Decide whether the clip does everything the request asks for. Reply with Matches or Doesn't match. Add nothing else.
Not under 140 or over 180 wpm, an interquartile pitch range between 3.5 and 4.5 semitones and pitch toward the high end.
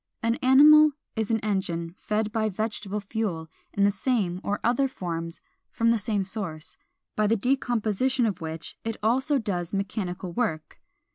Matches